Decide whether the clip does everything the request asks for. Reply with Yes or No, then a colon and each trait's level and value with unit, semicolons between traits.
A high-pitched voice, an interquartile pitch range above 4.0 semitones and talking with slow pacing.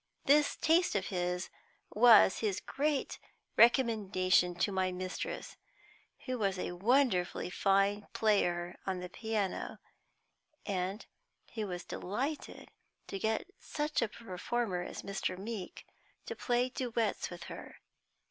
Yes: high, 205 Hz; average, 4.6 semitones; slow, 120 wpm